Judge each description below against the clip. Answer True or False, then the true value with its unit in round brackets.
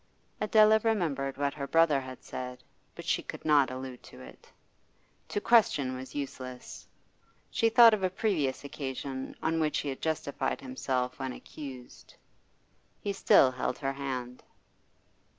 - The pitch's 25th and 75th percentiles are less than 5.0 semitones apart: False (5.3 semitones)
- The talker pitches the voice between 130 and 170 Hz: True (140 Hz)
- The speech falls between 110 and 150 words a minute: True (145 wpm)